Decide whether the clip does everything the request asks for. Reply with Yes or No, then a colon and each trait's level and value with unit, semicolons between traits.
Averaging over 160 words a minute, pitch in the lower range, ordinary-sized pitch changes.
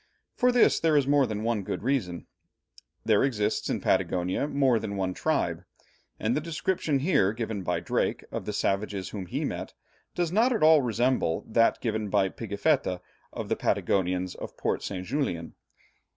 No: average, 170 wpm; low, 110 Hz; wide, 6.6 semitones